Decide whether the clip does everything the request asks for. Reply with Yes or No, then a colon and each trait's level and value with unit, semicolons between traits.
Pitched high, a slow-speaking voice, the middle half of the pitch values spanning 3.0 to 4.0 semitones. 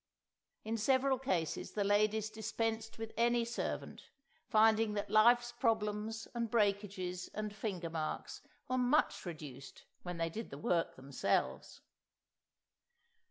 Yes: high, 215 Hz; slow, 115 wpm; average, 3.7 semitones